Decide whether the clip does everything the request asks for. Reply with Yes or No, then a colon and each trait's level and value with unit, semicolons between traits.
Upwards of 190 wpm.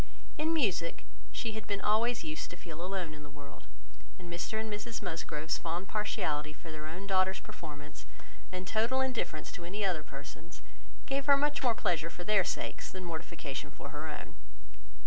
No: average, 180 wpm